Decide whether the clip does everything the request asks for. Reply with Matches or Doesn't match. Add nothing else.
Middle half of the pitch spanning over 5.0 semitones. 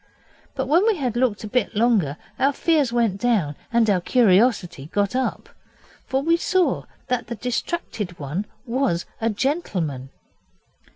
Matches